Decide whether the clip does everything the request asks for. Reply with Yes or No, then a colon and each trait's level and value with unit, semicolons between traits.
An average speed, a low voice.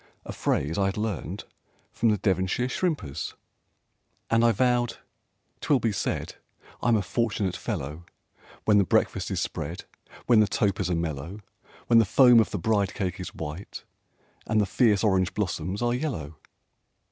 Yes: average, 160 wpm; low, 105 Hz